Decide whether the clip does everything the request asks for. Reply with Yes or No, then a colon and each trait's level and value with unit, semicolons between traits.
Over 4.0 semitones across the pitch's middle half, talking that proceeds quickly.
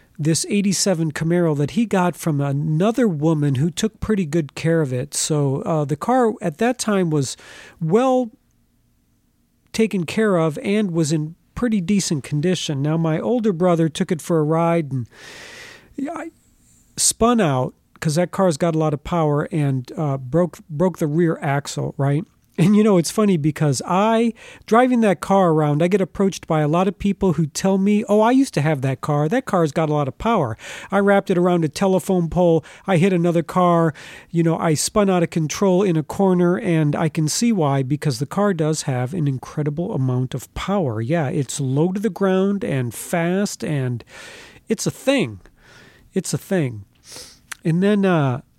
No: average, 4.7 semitones; average, 190 wpm